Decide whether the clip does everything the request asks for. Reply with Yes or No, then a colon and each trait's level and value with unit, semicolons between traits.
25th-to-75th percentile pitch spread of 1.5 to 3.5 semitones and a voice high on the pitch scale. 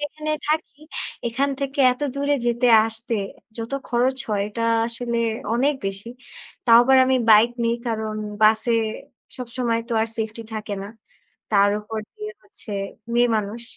Yes: average, 3.1 semitones; high, 235 Hz